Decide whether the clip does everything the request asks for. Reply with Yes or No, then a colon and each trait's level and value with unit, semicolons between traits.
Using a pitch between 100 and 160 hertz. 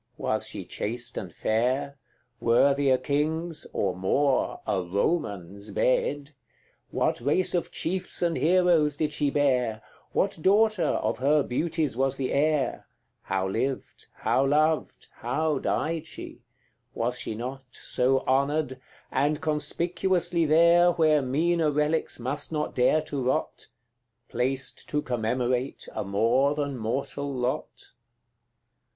Yes: medium, 140 Hz